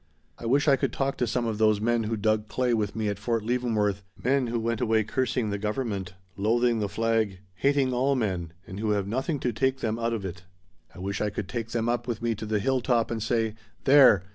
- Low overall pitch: Yes, low, 115 Hz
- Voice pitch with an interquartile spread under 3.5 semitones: Yes, average, 2.8 semitones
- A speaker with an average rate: No, fast, 240 wpm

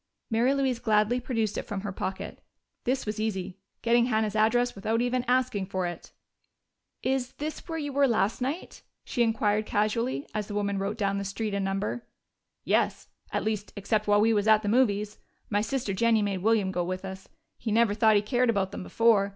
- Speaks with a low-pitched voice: No, high, 215 Hz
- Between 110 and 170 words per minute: No, average, 200 wpm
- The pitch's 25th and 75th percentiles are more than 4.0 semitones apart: No, average, 2.9 semitones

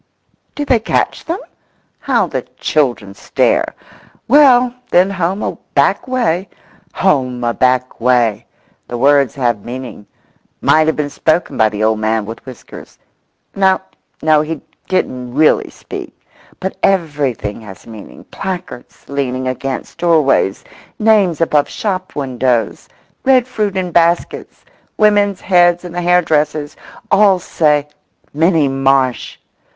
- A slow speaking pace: Yes, slow, 115 wpm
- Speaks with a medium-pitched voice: Yes, medium, 150 Hz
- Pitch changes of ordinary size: No, wide, 6.6 semitones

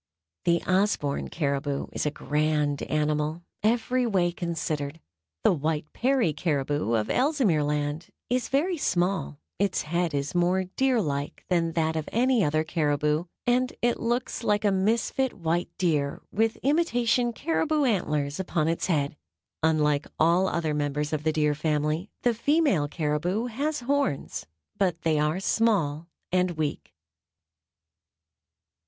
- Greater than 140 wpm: No, slow, 135 wpm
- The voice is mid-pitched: Yes, medium, 170 Hz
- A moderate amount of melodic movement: No, wide, 7.0 semitones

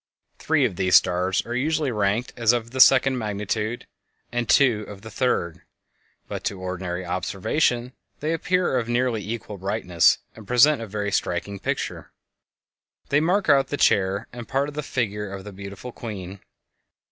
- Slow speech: No, average, 170 wpm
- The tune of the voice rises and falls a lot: No, average, 4.5 semitones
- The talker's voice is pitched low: Yes, low, 110 Hz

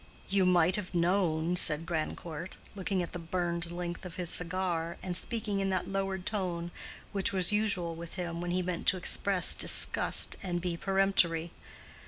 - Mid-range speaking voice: Yes, medium, 180 Hz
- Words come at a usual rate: Yes, average, 170 wpm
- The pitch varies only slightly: Yes, narrow, 2.1 semitones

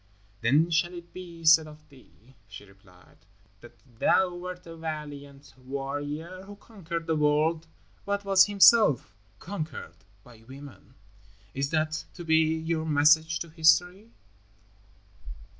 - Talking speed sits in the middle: No, slow, 125 wpm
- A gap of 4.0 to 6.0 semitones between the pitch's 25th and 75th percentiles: No, average, 3.6 semitones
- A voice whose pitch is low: No, medium, 160 Hz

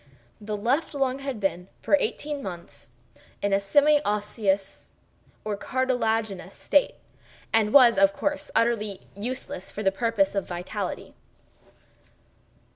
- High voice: Yes, high, 215 Hz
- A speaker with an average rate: No, slow, 120 wpm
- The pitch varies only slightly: No, average, 4.8 semitones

